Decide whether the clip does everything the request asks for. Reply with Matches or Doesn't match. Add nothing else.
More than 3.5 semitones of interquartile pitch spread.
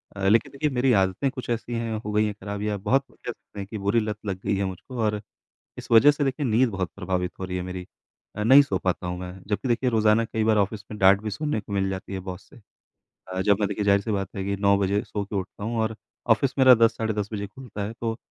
Doesn't match